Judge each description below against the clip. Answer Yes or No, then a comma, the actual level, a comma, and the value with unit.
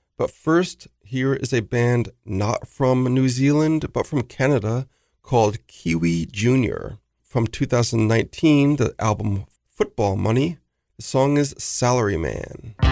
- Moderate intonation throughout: Yes, average, 4.1 semitones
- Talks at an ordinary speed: No, slow, 125 wpm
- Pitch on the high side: No, low, 125 Hz